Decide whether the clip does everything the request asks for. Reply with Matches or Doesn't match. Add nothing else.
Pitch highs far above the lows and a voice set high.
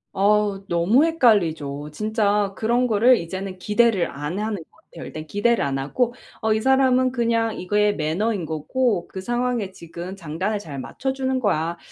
Matches